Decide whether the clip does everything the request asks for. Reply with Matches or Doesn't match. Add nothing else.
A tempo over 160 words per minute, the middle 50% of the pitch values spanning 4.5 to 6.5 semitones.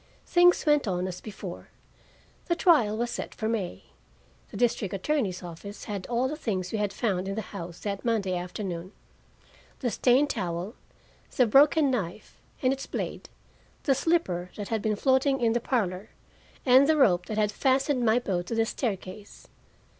Matches